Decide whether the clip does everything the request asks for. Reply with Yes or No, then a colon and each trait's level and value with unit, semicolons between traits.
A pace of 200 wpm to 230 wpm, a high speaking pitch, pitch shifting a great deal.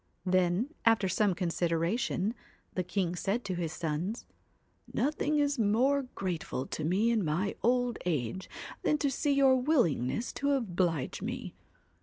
No: average, 145 wpm; high, 200 Hz; wide, 6.4 semitones